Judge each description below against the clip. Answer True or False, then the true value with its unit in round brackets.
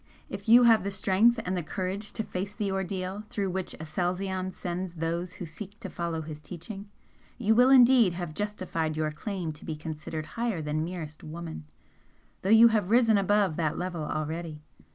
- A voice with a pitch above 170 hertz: True (185 Hz)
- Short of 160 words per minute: False (180 wpm)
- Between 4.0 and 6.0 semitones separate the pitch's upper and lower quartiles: True (4.3 semitones)